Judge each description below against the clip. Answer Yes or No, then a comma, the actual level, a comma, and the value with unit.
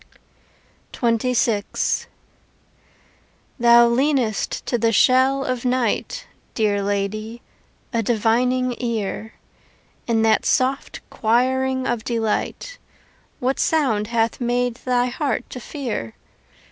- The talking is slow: Yes, slow, 95 wpm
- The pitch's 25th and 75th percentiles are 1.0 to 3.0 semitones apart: Yes, narrow, 2.4 semitones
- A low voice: No, high, 240 Hz